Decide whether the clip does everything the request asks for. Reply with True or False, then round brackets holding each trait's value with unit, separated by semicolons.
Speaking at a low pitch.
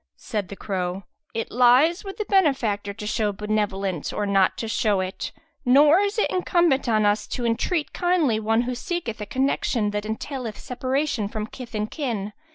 False (225 Hz)